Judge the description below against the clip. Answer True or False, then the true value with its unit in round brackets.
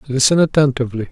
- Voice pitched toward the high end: False (135 Hz)